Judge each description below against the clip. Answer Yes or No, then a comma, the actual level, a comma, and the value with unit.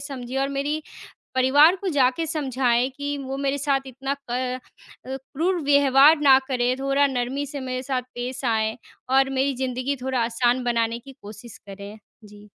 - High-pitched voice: Yes, very high, 265 Hz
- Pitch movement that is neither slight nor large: No, narrow, 2.3 semitones